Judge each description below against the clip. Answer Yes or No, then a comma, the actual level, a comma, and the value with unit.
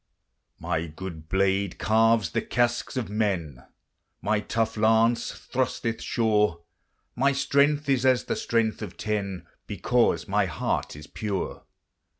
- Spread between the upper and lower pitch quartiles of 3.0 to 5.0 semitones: Yes, average, 3.6 semitones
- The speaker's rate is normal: No, slow, 130 wpm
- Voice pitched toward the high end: No, low, 110 Hz